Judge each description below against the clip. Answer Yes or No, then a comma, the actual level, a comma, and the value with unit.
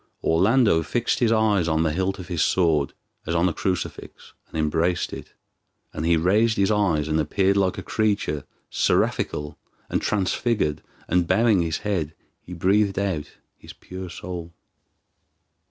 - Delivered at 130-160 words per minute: Yes, average, 155 wpm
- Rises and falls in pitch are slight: No, average, 3.7 semitones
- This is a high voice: No, very low, 90 Hz